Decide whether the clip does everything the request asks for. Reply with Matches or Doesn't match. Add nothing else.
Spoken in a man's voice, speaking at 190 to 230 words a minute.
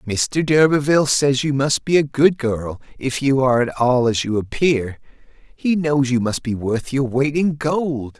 Matches